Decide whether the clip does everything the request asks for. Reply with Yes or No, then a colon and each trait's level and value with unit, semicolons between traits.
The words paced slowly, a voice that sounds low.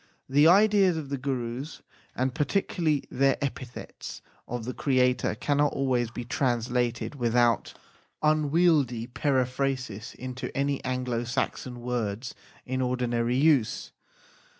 Yes: slow, 120 wpm; low, 130 Hz